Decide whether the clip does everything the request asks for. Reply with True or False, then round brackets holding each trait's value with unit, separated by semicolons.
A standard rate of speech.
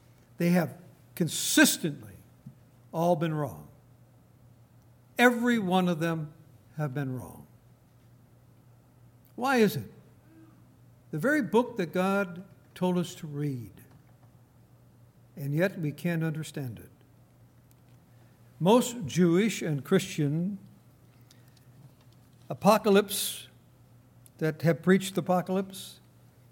False (95 wpm)